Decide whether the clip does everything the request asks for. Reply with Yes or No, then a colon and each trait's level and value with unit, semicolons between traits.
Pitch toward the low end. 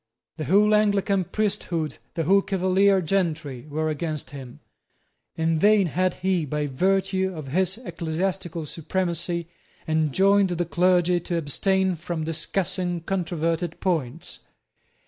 No: medium, 175 Hz